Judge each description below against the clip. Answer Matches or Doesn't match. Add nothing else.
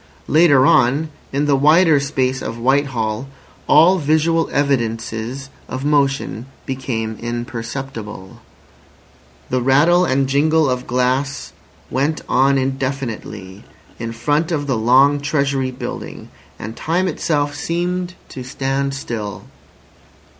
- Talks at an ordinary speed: Doesn't match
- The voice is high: Doesn't match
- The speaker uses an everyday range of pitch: Matches